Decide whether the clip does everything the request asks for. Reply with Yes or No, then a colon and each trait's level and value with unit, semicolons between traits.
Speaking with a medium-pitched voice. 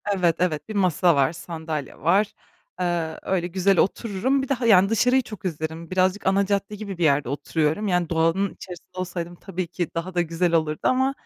Yes: medium, 180 Hz